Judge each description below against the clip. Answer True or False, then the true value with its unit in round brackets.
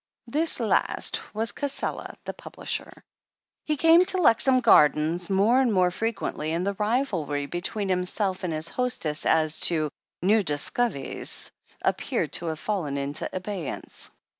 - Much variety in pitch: True (6.6 semitones)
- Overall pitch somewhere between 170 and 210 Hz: True (190 Hz)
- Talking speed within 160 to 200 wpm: False (140 wpm)